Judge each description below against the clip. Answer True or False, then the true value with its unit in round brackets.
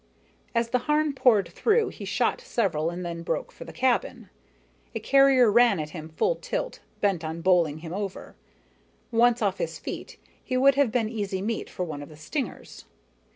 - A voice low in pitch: False (220 Hz)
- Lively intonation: True (7.3 semitones)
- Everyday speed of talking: True (185 wpm)